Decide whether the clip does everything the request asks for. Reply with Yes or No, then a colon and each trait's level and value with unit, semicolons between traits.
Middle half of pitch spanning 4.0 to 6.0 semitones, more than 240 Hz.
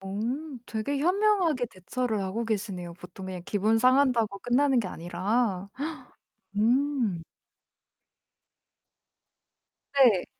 No: wide, 5.4 semitones; high, 225 Hz